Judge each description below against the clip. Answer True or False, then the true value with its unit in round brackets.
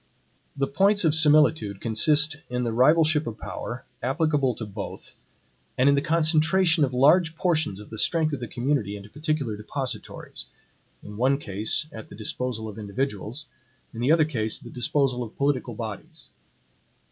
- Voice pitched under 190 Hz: True (135 Hz)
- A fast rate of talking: False (165 wpm)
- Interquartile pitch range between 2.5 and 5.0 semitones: False (5.5 semitones)